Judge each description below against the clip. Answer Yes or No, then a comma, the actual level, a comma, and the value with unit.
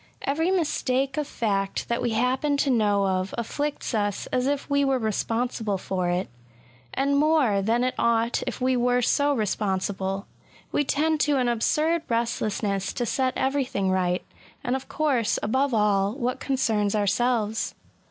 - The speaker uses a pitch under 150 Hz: No, high, 240 Hz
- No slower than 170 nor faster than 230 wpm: No, average, 160 wpm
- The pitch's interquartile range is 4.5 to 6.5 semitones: Yes, average, 4.9 semitones